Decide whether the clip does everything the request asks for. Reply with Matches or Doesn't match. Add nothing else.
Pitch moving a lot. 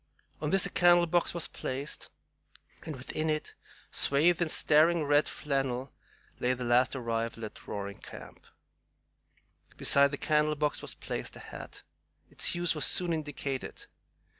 Doesn't match